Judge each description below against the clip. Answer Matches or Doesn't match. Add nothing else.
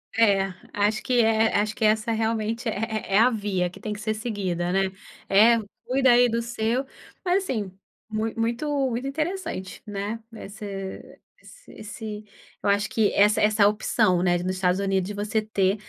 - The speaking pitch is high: Matches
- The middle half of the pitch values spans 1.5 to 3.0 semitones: Matches